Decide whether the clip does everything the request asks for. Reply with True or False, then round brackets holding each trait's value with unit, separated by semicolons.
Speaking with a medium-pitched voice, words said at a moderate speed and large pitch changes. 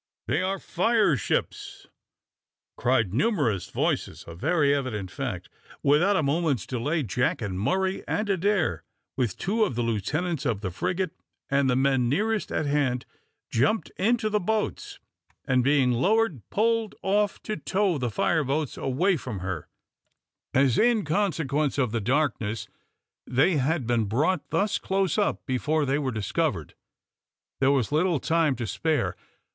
True (145 Hz; 150 wpm; 7.2 semitones)